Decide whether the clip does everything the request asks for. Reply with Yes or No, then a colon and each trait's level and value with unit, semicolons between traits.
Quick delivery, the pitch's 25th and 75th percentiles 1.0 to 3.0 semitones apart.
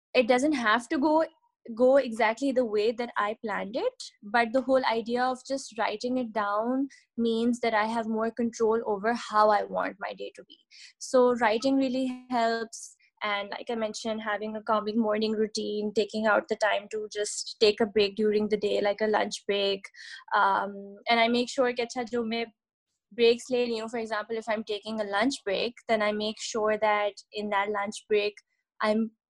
No: average, 195 wpm; narrow, 2.6 semitones